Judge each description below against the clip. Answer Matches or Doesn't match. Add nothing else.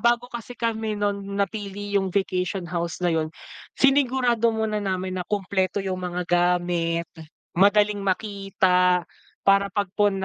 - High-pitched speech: Matches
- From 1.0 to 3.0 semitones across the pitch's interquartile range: Matches